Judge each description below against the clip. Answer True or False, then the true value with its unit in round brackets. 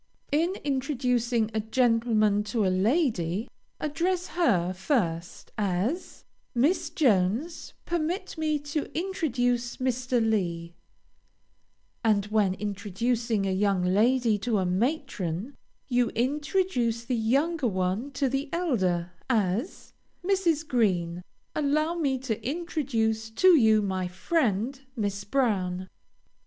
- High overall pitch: True (235 Hz)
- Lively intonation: True (6.2 semitones)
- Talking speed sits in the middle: False (110 wpm)